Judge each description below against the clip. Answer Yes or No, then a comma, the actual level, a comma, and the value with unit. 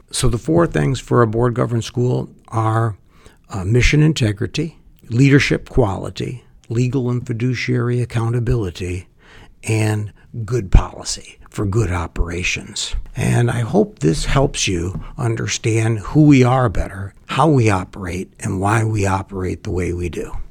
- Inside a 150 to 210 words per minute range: No, average, 140 wpm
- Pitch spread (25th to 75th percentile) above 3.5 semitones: Yes, average, 4.5 semitones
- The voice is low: Yes, low, 115 Hz